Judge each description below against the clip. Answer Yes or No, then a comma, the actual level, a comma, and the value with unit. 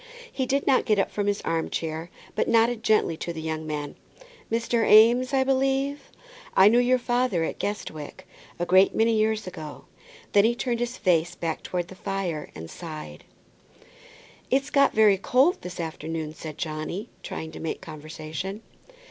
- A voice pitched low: No, high, 195 Hz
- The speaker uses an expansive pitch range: Yes, wide, 6.9 semitones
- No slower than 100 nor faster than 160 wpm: No, average, 170 wpm